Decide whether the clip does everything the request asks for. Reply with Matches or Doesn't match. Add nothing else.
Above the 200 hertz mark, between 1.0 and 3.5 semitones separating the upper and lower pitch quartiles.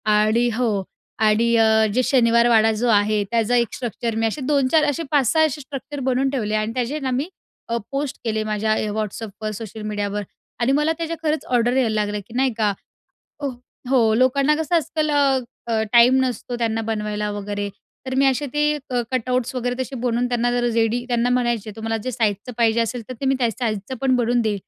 Matches